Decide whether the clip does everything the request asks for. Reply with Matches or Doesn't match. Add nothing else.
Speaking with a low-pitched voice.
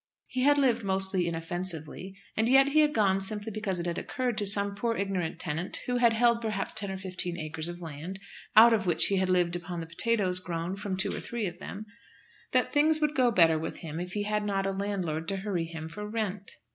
Doesn't match